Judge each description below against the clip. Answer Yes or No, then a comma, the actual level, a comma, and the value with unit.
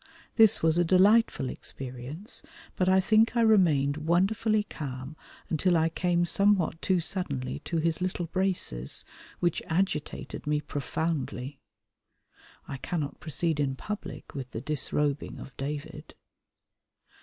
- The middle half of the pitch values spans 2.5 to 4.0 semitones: No, average, 4.7 semitones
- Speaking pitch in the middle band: Yes, medium, 160 Hz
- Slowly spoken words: Yes, slow, 125 wpm